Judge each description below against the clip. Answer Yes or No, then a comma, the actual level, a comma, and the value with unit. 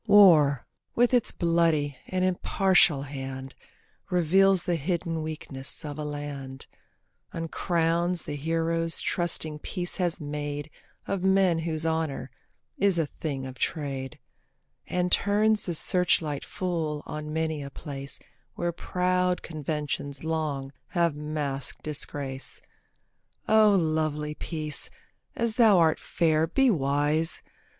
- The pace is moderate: No, slow, 120 wpm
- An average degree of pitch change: Yes, average, 3.4 semitones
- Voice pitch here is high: No, medium, 160 Hz